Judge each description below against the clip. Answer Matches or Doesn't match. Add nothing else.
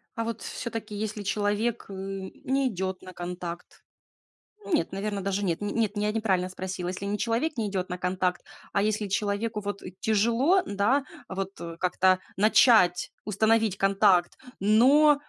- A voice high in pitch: Matches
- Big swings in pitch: Doesn't match